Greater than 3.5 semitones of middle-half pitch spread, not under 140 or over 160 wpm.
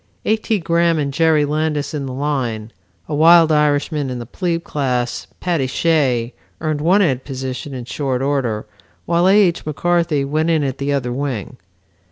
No: average, 3.9 semitones; average, 175 wpm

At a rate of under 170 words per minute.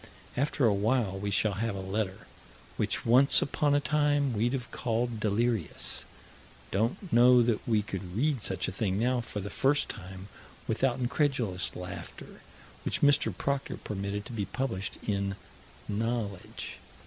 Yes: average, 150 wpm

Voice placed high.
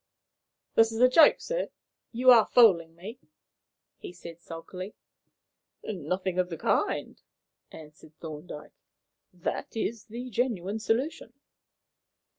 Yes: high, 195 Hz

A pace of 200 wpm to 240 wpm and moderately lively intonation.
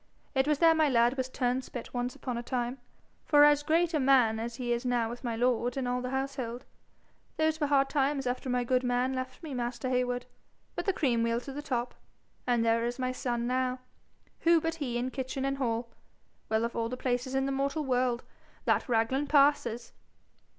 No: fast, 205 wpm; narrow, 2.3 semitones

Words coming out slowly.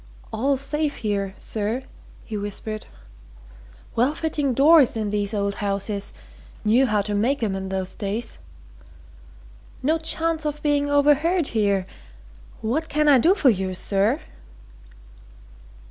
Yes: slow, 130 wpm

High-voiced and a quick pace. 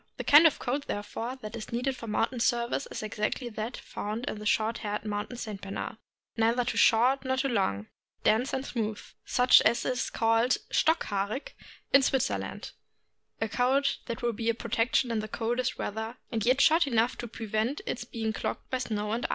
Yes: high, 230 Hz; fast, 215 wpm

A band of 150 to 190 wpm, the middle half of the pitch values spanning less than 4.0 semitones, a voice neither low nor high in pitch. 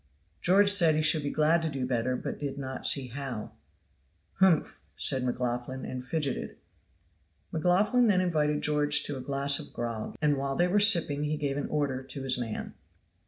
Yes: average, 180 wpm; average, 3.4 semitones; medium, 145 Hz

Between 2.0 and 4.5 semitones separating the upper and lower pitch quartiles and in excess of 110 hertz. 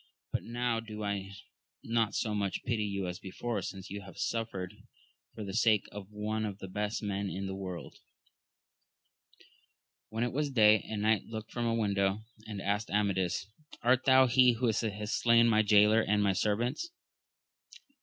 No: narrow, 2.4 semitones; low, 105 Hz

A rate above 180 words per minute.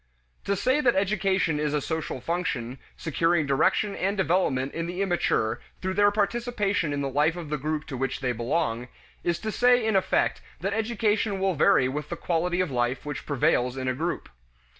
Yes: average, 190 wpm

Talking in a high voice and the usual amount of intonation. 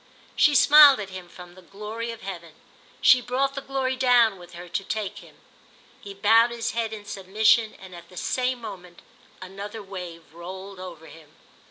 Yes: high, 200 Hz; average, 4.5 semitones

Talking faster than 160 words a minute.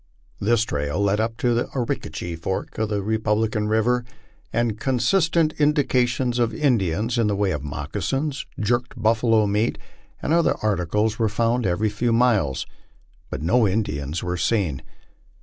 No: average, 150 wpm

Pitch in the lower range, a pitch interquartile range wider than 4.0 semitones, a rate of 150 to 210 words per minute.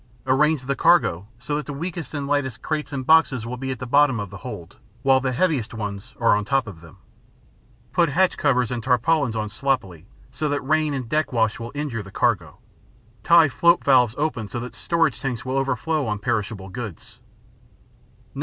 Yes: low, 130 Hz; average, 4.9 semitones; average, 190 wpm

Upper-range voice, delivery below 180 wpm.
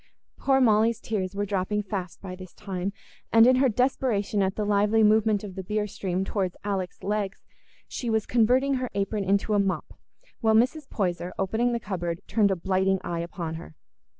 No: high, 205 Hz; average, 185 wpm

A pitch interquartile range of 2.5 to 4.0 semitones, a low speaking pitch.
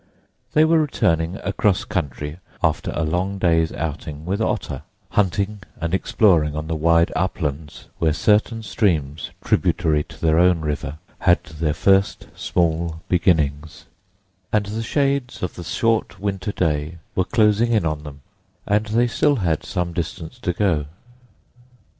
No: average, 4.6 semitones; very low, 85 Hz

